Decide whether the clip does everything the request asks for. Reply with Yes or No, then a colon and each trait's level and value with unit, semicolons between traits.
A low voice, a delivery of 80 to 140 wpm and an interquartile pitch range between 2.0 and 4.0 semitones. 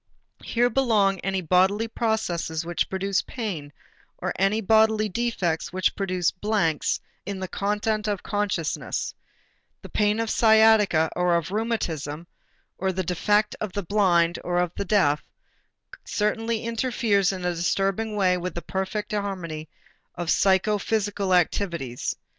No: high, 195 Hz; slow, 135 wpm; average, 3.3 semitones